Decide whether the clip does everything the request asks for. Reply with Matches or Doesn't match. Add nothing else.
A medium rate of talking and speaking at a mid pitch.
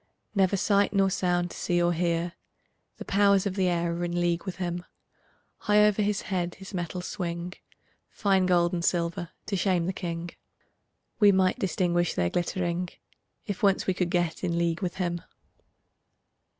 Matches